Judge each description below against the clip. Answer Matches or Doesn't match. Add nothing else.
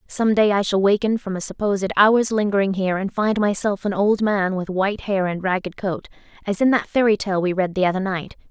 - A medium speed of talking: Doesn't match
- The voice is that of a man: Doesn't match